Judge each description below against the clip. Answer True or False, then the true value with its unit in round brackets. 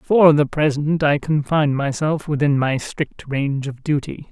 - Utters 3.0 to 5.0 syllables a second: True (4.5 syllables/s)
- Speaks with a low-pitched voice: False (145 Hz)